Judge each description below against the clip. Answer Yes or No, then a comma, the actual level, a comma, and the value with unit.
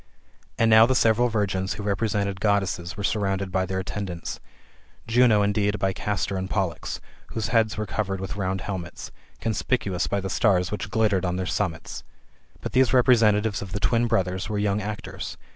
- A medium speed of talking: Yes, average, 175 wpm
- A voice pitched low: Yes, low, 100 Hz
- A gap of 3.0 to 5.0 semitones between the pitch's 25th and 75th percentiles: No, narrow, 2.5 semitones